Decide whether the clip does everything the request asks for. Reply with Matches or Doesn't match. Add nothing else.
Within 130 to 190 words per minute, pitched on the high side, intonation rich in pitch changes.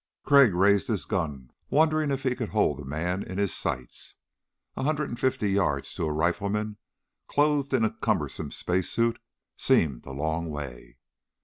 Doesn't match